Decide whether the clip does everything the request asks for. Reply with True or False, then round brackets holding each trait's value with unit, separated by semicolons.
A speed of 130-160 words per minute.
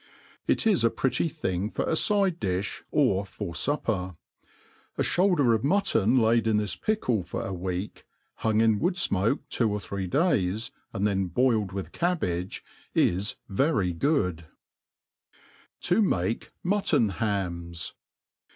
True (140 wpm)